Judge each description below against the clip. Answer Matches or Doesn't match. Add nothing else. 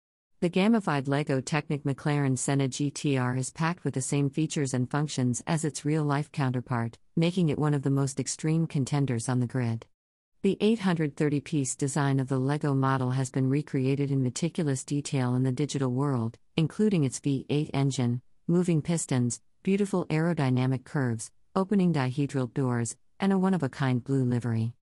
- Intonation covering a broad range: Doesn't match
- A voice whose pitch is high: Doesn't match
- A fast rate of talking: Doesn't match